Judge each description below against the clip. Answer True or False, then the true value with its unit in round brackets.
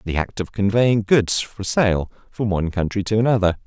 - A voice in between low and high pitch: False (100 Hz)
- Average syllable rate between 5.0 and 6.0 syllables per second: True (5.1 syllables/s)